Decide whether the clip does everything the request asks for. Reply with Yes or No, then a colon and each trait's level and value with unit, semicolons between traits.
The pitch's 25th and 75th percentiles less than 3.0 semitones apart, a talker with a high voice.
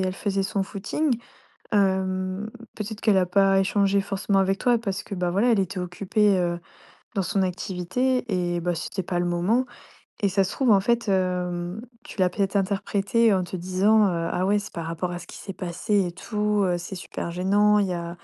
Yes: narrow, 2.4 semitones; high, 195 Hz